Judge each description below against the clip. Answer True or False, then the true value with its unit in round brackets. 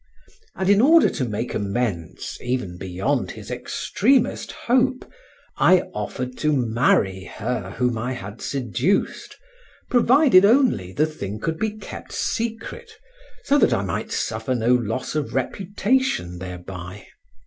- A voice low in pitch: True (125 Hz)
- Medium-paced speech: False (130 wpm)